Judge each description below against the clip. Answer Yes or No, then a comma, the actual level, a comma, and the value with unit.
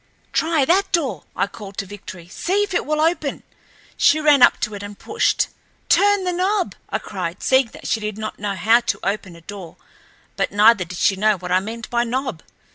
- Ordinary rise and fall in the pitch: No, wide, 7.7 semitones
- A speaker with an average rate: No, fast, 210 wpm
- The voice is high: Yes, high, 225 Hz